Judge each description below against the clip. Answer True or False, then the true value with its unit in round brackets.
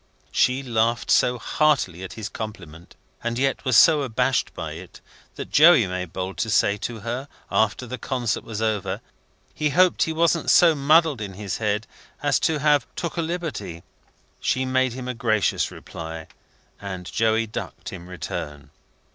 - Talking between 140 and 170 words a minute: True (165 wpm)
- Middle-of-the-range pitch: False (115 Hz)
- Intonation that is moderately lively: False (6.0 semitones)